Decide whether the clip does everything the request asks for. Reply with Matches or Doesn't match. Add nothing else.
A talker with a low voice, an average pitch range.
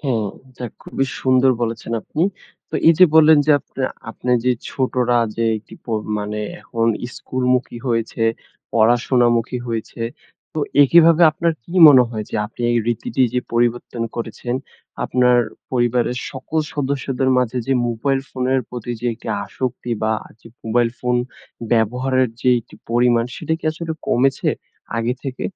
Doesn't match